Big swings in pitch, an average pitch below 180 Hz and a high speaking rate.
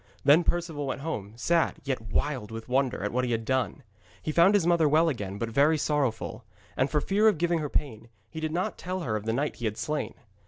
Yes: wide, 5.9 semitones; medium, 140 Hz; fast, 235 wpm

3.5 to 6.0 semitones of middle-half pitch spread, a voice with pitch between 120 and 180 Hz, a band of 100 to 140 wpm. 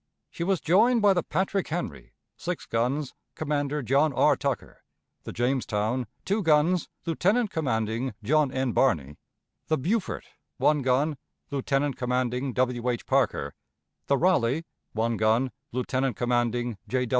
Yes: average, 4.5 semitones; low, 135 Hz; slow, 135 wpm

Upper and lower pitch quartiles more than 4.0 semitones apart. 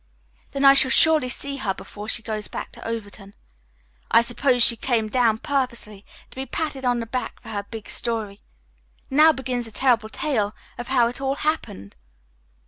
No: average, 3.6 semitones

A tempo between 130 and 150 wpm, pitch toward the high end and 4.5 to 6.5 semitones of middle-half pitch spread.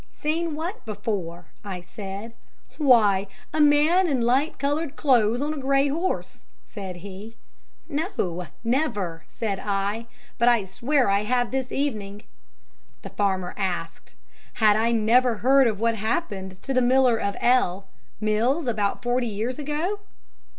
Yes: average, 145 wpm; high, 230 Hz; wide, 5.5 semitones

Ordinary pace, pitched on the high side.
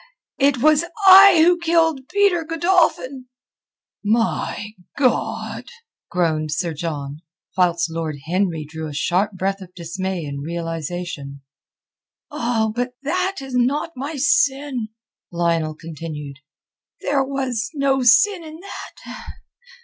No: slow, 115 wpm; high, 225 Hz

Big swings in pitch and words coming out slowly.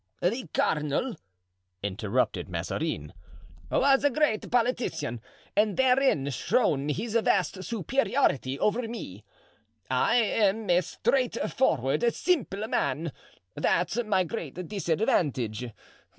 Yes: wide, 8.8 semitones; slow, 95 wpm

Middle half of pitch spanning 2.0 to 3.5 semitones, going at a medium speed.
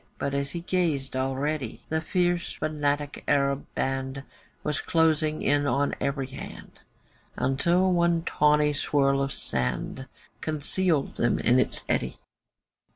No: average, 2.7 semitones; slow, 125 wpm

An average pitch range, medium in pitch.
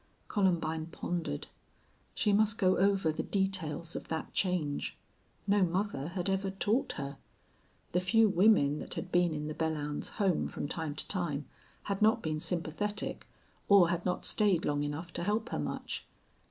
Yes: average, 4.1 semitones; medium, 175 Hz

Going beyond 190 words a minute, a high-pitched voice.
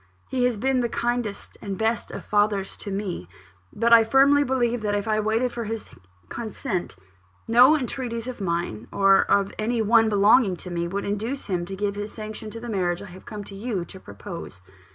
Yes: average, 200 wpm; high, 215 Hz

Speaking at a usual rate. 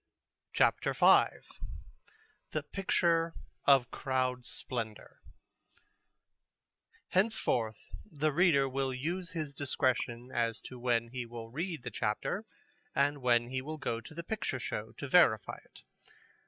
No: slow, 125 wpm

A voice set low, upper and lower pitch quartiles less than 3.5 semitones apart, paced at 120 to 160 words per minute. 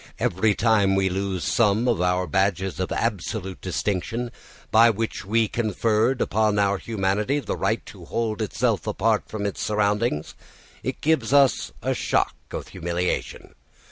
Yes: low, 105 Hz; average, 3.0 semitones; average, 145 wpm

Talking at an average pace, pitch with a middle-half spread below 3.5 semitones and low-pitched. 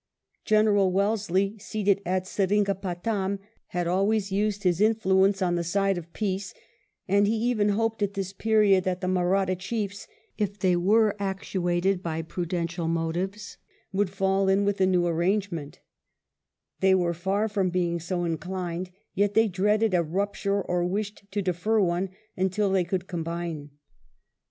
No: average, 150 wpm; narrow, 2.4 semitones; high, 190 Hz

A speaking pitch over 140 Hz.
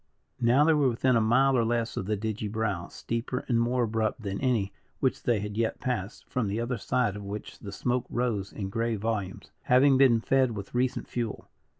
No: low, 115 Hz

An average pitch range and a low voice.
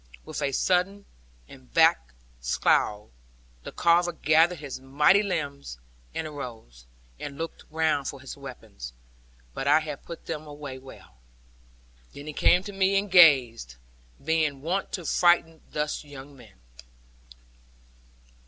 No: average, 4.1 semitones; medium, 145 Hz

